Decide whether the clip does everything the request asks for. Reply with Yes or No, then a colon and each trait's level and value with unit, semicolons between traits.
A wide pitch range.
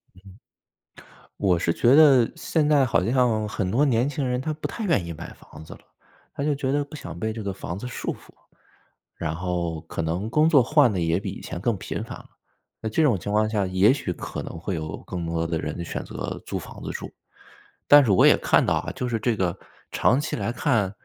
Yes: wide, 7.0 semitones